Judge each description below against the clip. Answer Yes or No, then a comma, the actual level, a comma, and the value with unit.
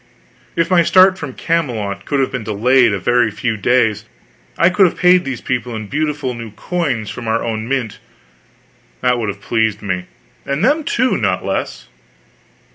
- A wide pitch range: Yes, wide, 6.2 semitones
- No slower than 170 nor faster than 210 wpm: Yes, average, 180 wpm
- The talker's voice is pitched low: Yes, low, 125 Hz